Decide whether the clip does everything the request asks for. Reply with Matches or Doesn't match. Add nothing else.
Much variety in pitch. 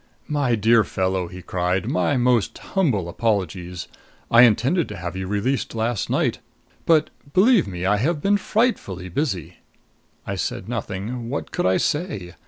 Matches